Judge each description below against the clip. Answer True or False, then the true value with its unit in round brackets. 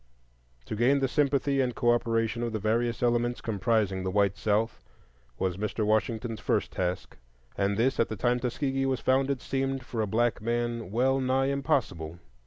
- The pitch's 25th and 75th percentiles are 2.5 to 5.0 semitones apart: True (3.3 semitones)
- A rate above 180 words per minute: False (170 wpm)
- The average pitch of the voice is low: True (120 Hz)